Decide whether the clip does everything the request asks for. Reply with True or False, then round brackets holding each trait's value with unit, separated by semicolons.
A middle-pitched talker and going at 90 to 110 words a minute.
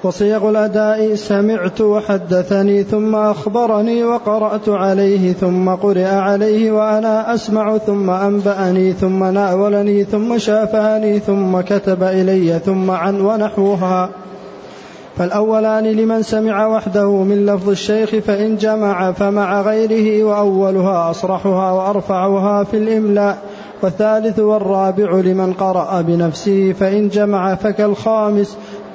False (205 Hz; 100 wpm)